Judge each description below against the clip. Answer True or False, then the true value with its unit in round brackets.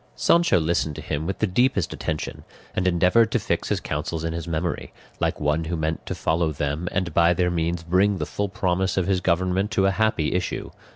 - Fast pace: True (215 wpm)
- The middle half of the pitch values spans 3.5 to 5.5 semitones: False (3.0 semitones)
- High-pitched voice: False (90 Hz)